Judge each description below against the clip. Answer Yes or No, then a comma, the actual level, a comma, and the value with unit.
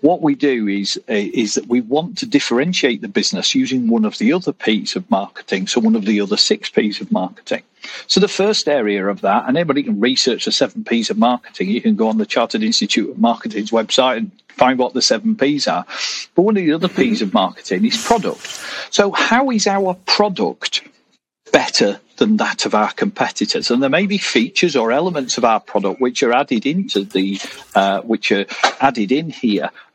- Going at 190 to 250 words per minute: Yes, fast, 205 wpm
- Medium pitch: Yes, medium, 155 Hz